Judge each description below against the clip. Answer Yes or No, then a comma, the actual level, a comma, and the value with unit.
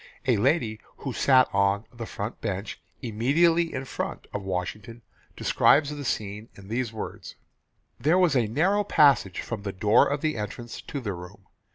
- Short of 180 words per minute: Yes, average, 165 wpm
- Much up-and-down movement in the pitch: Yes, wide, 5.7 semitones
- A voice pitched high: No, low, 115 Hz